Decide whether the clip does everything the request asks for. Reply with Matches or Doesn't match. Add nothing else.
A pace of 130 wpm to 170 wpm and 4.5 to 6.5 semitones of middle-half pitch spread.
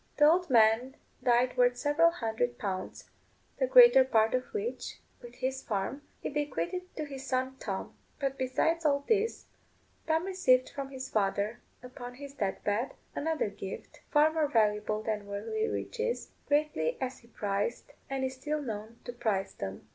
Matches